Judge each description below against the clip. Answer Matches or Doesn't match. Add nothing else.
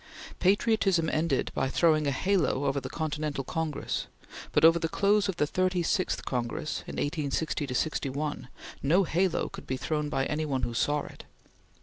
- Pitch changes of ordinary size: Matches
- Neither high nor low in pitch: Matches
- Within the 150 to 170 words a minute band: Matches